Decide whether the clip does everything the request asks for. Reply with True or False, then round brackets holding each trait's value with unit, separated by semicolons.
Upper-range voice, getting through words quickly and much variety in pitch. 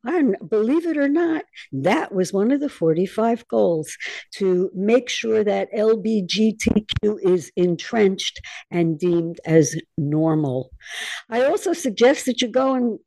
False (210 Hz; 140 wpm; 6.0 semitones)